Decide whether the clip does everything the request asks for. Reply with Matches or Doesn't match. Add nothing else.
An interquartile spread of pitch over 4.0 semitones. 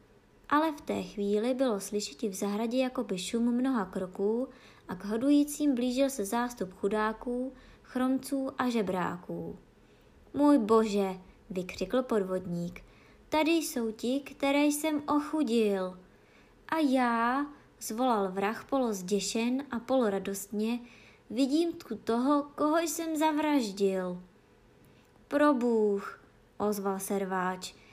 Matches